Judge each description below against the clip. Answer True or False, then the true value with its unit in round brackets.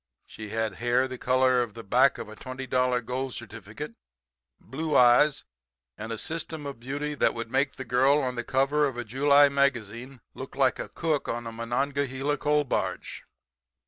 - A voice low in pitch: True (130 Hz)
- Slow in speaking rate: False (180 wpm)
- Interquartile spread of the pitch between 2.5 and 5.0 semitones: True (2.9 semitones)